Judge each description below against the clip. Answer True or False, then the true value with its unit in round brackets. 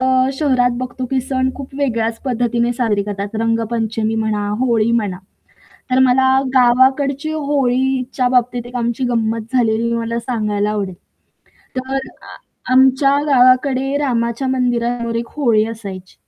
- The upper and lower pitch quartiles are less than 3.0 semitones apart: True (2.5 semitones)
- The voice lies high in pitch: True (245 Hz)